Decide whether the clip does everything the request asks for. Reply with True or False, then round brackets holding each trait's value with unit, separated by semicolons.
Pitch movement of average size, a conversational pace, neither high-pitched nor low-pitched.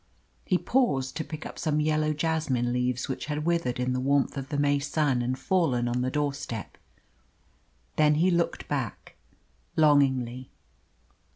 True (3.3 semitones; 155 wpm; 145 Hz)